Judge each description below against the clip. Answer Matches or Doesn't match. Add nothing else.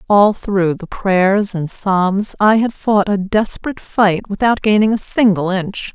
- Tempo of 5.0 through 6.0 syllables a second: Doesn't match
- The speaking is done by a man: Doesn't match